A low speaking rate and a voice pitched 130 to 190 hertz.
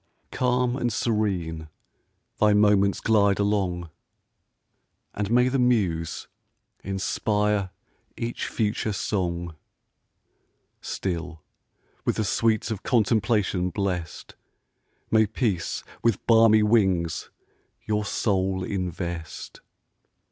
No: slow, 90 wpm; low, 105 Hz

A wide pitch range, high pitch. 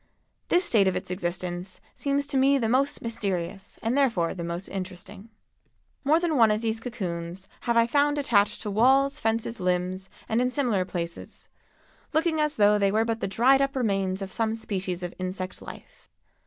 Yes: wide, 5.7 semitones; high, 220 Hz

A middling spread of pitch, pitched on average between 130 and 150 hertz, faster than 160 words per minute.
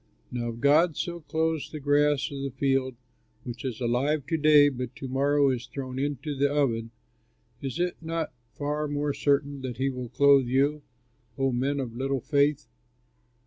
No: narrow, 2.2 semitones; medium, 140 Hz; average, 175 wpm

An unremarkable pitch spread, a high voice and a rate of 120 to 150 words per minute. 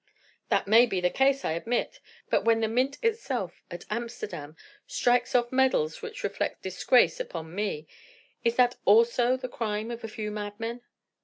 No: average, 3.3 semitones; high, 230 Hz; average, 165 wpm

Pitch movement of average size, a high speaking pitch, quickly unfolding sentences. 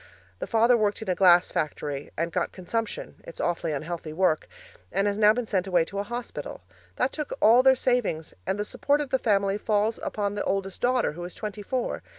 Yes: average, 4.6 semitones; high, 205 Hz; fast, 210 wpm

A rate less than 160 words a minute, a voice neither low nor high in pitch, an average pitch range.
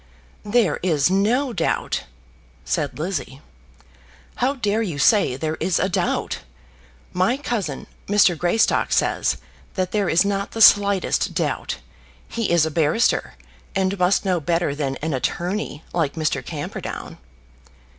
Yes: slow, 135 wpm; medium, 180 Hz; average, 4.4 semitones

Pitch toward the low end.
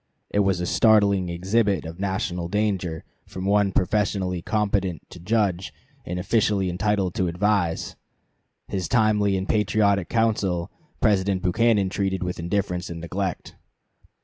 Yes: very low, 95 Hz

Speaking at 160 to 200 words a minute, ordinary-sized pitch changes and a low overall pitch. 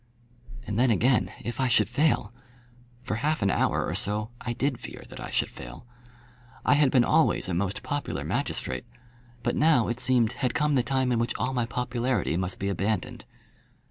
Yes: average, 190 wpm; average, 3.5 semitones; low, 120 Hz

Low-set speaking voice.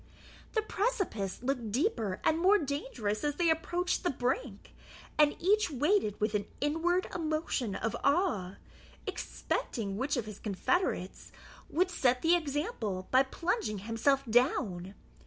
No: very high, 275 Hz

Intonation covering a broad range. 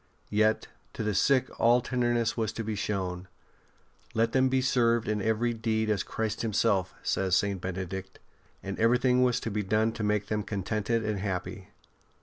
No: average, 2.8 semitones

